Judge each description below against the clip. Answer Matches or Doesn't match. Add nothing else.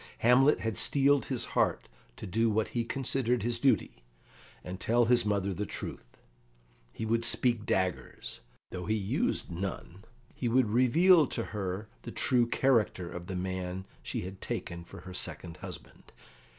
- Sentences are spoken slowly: Doesn't match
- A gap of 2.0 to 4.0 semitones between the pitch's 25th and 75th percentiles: Doesn't match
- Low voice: Matches